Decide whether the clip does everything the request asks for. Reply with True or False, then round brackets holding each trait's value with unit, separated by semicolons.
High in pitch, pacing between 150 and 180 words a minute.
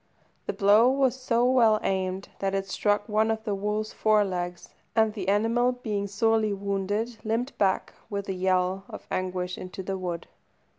True (205 Hz; 170 wpm)